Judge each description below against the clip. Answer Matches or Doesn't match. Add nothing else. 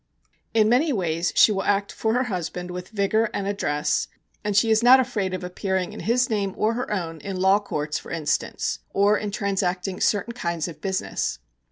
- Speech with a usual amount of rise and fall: Matches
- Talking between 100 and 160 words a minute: Doesn't match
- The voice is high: Matches